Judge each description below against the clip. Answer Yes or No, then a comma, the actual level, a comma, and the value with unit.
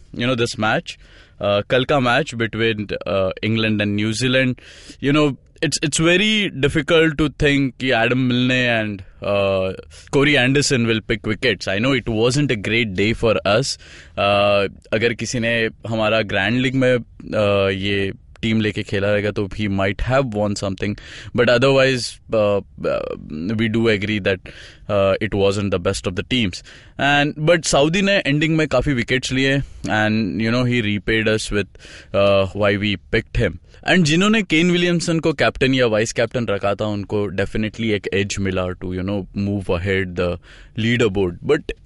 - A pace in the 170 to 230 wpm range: No, average, 160 wpm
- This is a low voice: Yes, low, 110 Hz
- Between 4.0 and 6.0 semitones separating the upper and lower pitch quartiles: Yes, average, 4.4 semitones